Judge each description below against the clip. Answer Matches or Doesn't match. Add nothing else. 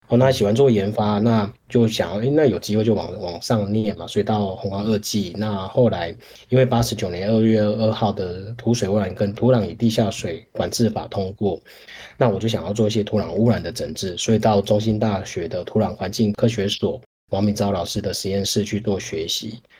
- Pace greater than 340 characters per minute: Doesn't match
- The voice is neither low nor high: Doesn't match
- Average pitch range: Doesn't match